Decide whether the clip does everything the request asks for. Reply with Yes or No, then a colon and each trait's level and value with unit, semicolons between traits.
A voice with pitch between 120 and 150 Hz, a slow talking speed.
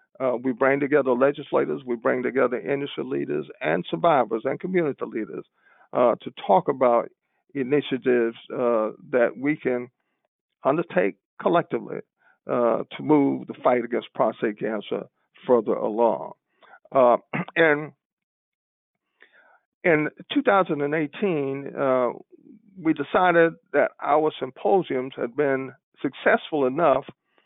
Yes: medium, 140 Hz; slow, 110 wpm